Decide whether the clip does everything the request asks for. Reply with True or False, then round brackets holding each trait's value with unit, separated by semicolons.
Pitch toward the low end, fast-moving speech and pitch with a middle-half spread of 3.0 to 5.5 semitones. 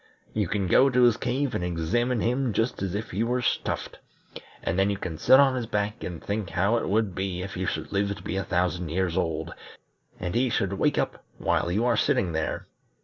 True (100 Hz; 225 wpm; 4.9 semitones)